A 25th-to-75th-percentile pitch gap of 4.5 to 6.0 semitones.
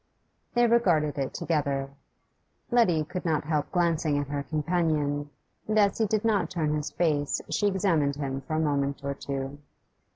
No: average, 3.8 semitones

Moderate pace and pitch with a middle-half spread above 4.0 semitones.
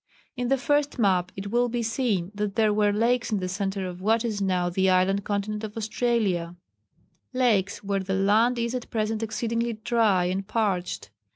No: average, 185 wpm; average, 3.3 semitones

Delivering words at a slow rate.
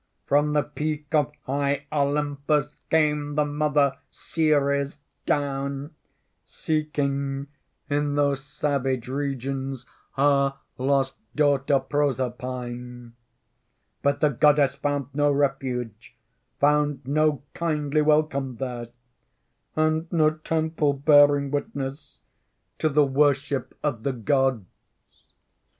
Yes: slow, 100 wpm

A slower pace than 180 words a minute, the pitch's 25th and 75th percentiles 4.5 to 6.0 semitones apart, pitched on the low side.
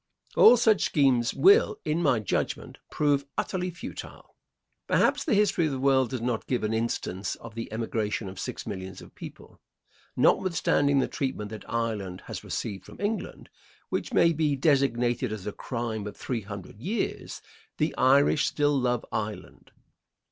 Yes: average, 160 wpm; average, 5.3 semitones; low, 125 Hz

